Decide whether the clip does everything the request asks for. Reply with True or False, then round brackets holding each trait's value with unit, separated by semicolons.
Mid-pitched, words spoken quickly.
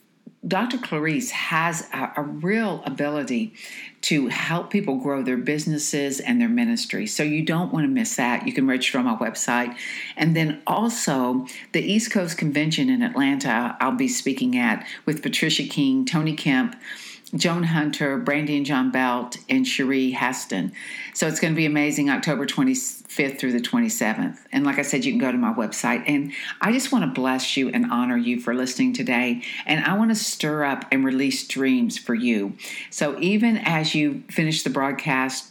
False (170 Hz; 180 wpm)